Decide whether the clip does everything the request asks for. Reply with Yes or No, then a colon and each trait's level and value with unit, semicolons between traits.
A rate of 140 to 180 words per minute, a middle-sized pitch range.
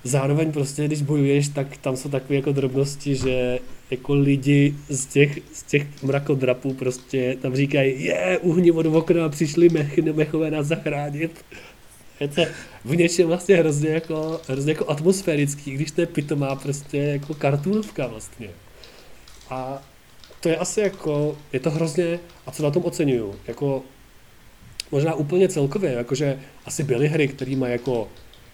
Yes: average, 150 wpm; average, 3.1 semitones